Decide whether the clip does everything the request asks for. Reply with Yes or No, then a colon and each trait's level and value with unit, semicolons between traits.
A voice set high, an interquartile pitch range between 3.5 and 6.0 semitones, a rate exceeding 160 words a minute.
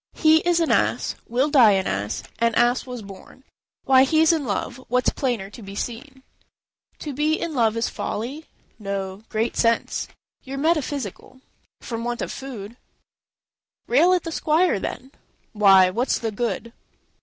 Yes: high, 245 Hz; average, 5.2 semitones; average, 170 wpm